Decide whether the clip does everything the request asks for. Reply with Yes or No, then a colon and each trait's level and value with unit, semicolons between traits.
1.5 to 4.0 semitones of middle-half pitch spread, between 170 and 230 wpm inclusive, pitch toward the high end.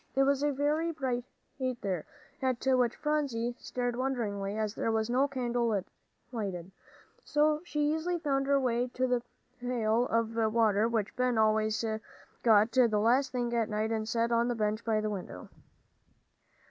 No: average, 3.3 semitones; average, 160 wpm; high, 240 Hz